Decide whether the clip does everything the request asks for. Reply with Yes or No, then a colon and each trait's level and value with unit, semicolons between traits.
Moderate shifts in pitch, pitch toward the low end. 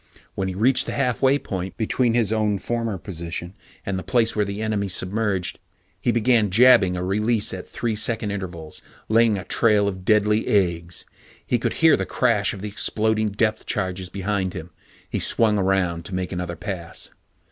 Yes: average, 3.0 semitones; low, 100 Hz